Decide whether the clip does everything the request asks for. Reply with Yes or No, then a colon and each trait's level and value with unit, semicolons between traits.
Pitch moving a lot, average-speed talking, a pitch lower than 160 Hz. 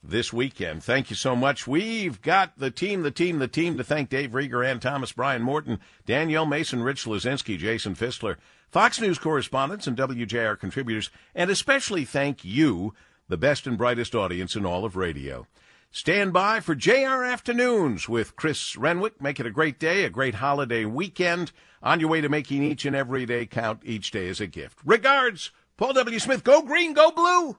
Yes: wide, 6.8 semitones; average, 190 wpm; medium, 140 Hz